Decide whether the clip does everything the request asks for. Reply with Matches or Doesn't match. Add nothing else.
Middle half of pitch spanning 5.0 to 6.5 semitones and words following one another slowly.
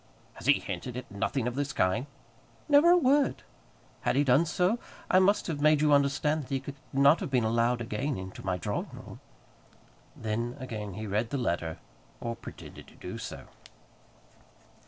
Doesn't match